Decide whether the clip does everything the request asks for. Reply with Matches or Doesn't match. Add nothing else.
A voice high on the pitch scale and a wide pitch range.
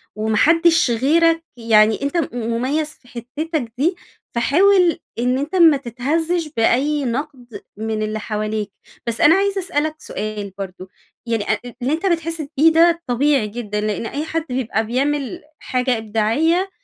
Matches